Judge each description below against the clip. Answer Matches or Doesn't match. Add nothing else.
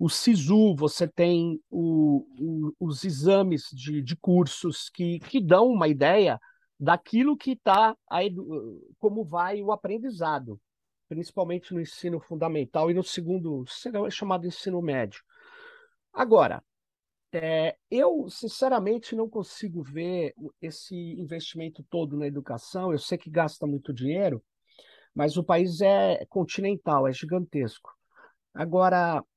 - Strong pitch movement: Doesn't match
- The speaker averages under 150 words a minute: Matches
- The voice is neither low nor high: Matches